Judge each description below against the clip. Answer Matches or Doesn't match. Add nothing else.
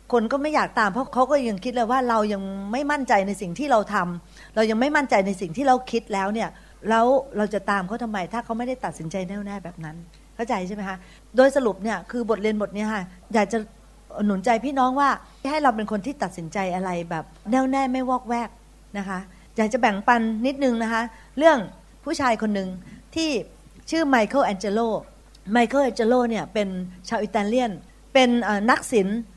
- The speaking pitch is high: Matches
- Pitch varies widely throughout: Doesn't match